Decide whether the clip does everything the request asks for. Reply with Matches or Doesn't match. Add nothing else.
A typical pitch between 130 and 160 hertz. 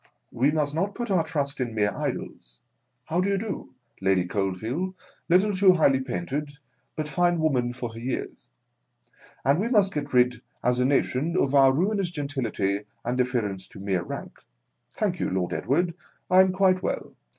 Matches